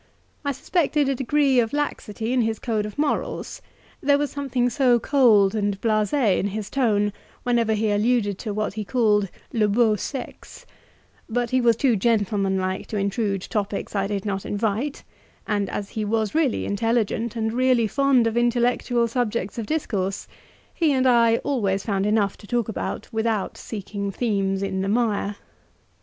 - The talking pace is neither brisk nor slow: Yes, average, 165 wpm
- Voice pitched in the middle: No, high, 220 Hz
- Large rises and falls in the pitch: No, average, 3.2 semitones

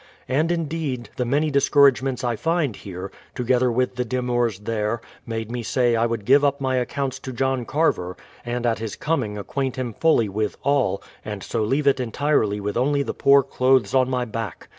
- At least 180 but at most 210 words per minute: Yes, average, 200 wpm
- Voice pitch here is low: Yes, low, 125 Hz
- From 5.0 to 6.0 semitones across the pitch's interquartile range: No, average, 3.4 semitones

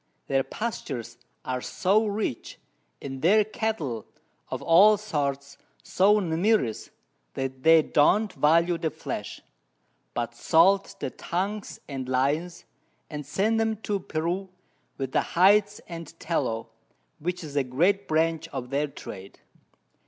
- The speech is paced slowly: Yes, slow, 130 wpm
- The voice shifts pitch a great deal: Yes, wide, 6.3 semitones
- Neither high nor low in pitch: Yes, medium, 165 Hz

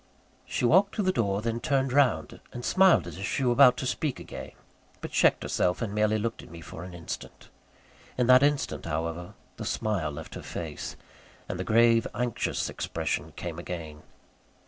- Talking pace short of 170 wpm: No, average, 185 wpm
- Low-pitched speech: Yes, low, 110 Hz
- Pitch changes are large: Yes, wide, 6.5 semitones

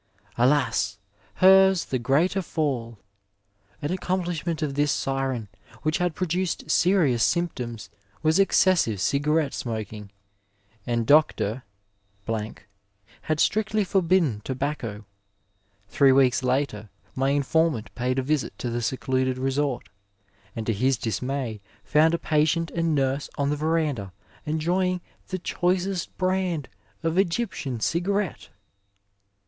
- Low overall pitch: No, medium, 145 Hz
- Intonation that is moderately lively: No, wide, 5.7 semitones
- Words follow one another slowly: Yes, slow, 110 wpm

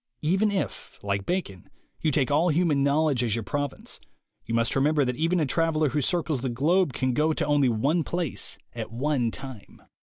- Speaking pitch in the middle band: Yes, medium, 145 Hz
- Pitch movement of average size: Yes, average, 4.2 semitones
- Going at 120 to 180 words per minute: No, average, 190 wpm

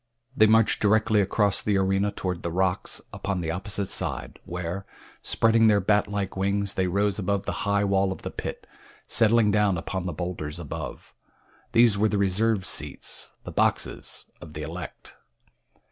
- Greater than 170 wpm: No, average, 165 wpm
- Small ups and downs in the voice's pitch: Yes, narrow, 2.3 semitones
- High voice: No, low, 100 Hz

